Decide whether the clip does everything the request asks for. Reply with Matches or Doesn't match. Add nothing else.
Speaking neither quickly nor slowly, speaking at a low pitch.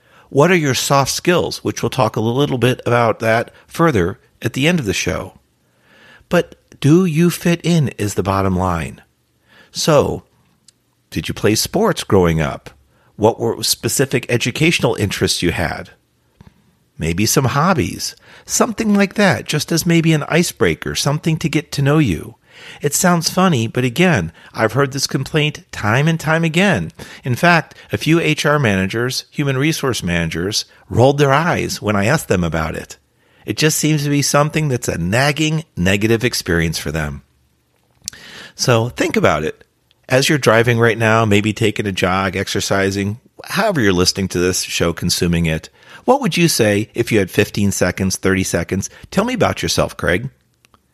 Matches